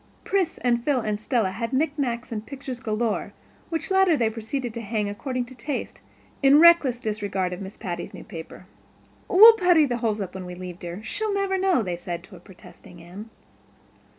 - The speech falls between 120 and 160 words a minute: No, average, 185 wpm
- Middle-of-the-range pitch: No, high, 230 Hz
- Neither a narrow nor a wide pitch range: No, wide, 6.5 semitones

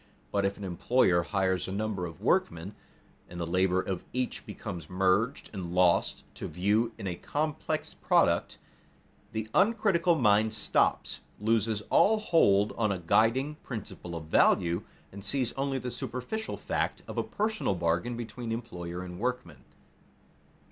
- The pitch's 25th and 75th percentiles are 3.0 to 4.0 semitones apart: No, wide, 5.6 semitones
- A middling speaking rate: Yes, average, 150 wpm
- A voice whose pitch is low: Yes, low, 105 Hz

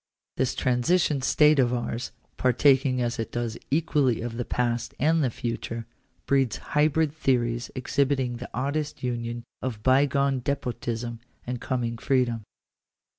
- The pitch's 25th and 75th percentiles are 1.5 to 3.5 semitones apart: Yes, average, 2.8 semitones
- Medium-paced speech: No, slow, 130 wpm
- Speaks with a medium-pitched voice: No, low, 125 Hz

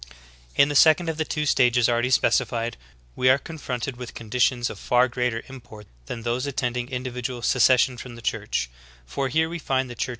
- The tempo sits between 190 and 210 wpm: Yes, average, 195 wpm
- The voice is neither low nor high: No, low, 125 Hz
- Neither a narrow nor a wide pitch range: No, narrow, 2.0 semitones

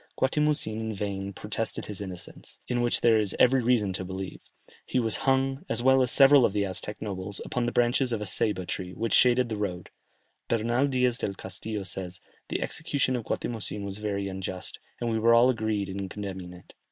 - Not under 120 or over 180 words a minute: No, average, 200 wpm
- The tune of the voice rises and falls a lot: No, average, 4.0 semitones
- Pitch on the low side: Yes, low, 110 Hz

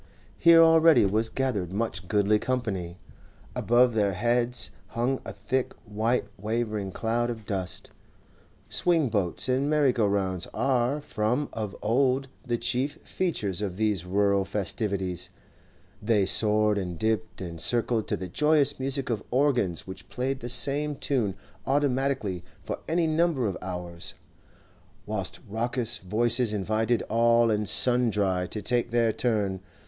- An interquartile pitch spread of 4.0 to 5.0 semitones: Yes, average, 4.3 semitones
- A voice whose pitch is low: Yes, low, 115 Hz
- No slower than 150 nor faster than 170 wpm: No, average, 140 wpm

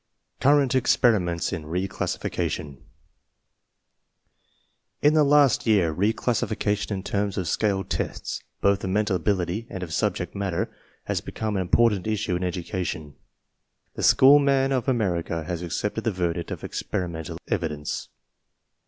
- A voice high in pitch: No, low, 100 Hz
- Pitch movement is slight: No, average, 4.4 semitones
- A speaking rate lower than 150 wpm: Yes, average, 140 wpm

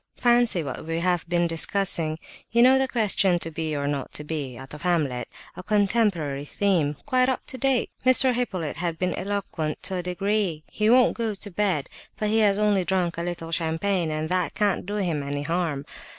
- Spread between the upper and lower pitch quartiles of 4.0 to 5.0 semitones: Yes, average, 4.7 semitones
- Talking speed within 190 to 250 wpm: Yes, average, 195 wpm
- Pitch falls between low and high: Yes, medium, 180 Hz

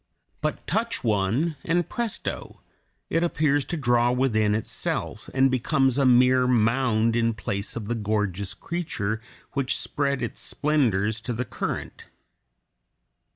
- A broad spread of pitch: No, average, 4.2 semitones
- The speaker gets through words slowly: Yes, slow, 130 wpm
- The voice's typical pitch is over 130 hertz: No, low, 125 Hz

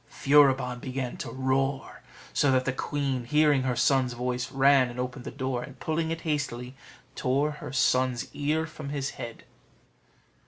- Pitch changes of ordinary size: No, narrow, 2.3 semitones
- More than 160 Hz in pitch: No, low, 135 Hz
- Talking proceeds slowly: No, average, 160 wpm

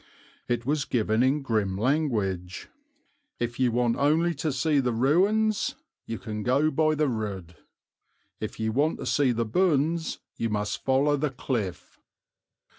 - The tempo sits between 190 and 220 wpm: No, average, 150 wpm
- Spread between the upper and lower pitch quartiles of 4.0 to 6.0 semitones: Yes, wide, 5.4 semitones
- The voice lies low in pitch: Yes, low, 130 Hz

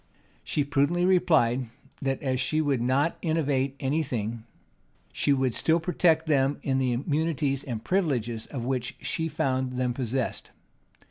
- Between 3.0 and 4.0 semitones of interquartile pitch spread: Yes, average, 3.7 semitones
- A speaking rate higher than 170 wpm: No, average, 145 wpm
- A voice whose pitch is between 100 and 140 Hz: Yes, low, 135 Hz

